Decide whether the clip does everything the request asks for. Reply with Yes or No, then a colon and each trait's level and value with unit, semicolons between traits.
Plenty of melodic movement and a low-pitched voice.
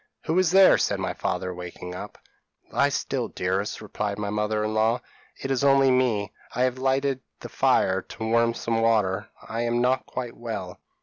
No: average, 3.9 semitones; low, 115 Hz